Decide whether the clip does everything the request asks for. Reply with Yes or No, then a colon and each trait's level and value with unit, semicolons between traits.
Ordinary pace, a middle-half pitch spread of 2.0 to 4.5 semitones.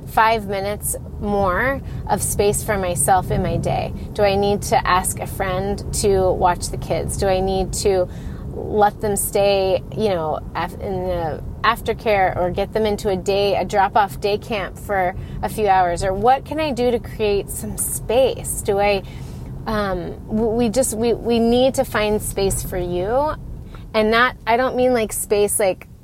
Yes: average, 180 wpm; average, 2.9 semitones